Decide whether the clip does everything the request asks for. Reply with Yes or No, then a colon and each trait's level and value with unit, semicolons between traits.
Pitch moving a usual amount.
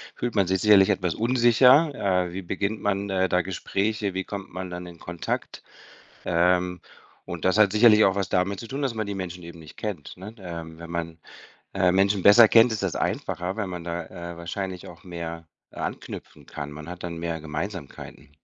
Yes: average, 3.0 semitones